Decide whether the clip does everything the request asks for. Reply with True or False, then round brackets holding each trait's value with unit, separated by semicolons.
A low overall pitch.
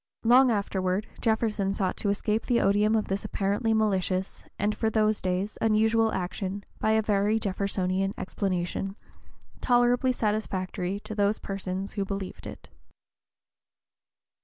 False (205 Hz)